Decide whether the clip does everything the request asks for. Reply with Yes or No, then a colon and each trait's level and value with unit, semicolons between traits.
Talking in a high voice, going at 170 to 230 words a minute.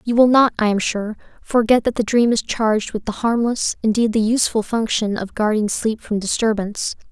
Yes: high, 220 Hz; average, 200 wpm